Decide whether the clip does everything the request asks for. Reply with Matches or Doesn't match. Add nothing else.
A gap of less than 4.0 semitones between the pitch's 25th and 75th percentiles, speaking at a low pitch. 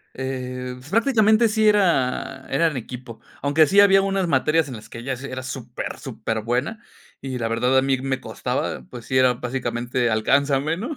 Doesn't match